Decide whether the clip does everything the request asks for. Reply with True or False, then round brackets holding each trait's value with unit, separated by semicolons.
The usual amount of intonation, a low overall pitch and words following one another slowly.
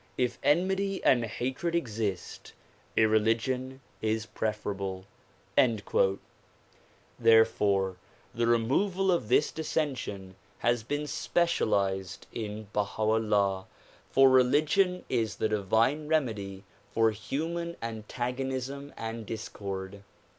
True (5.0 semitones; 115 Hz; 90 wpm)